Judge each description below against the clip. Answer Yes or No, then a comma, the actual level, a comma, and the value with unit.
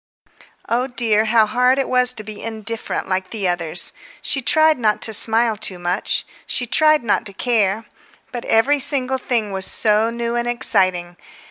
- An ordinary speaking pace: Yes, average, 170 wpm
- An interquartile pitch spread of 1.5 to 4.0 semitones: Yes, average, 3.2 semitones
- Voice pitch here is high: Yes, high, 225 Hz